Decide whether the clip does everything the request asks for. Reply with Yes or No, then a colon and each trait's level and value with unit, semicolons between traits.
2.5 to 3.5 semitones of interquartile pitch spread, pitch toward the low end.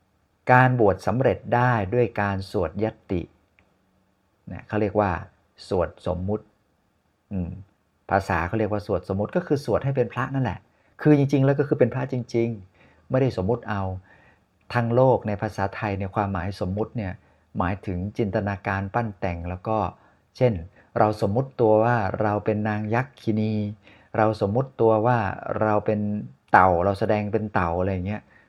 Yes: average, 3.1 semitones; low, 105 Hz